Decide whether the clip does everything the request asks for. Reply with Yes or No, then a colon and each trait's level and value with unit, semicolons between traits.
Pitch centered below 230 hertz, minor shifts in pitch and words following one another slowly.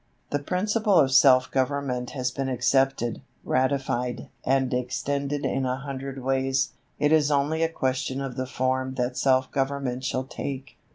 No: low, 135 Hz; narrow, 1.5 semitones; average, 155 wpm